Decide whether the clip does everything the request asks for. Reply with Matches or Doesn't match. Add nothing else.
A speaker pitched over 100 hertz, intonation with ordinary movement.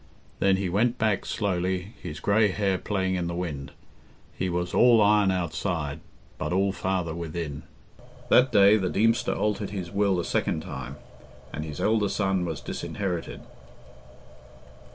Doesn't match